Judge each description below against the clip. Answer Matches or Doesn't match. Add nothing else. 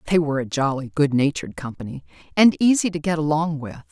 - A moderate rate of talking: Matches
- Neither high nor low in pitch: Matches